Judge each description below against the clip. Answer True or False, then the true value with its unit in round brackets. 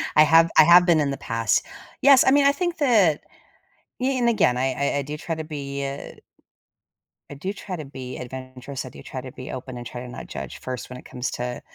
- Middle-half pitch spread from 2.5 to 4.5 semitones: False (5.2 semitones)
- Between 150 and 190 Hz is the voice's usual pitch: False (140 Hz)